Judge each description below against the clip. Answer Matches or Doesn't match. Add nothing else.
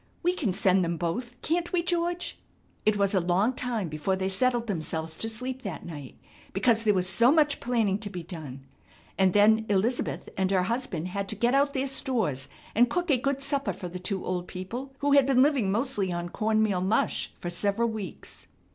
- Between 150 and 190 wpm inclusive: Doesn't match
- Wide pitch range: Matches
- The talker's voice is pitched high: Matches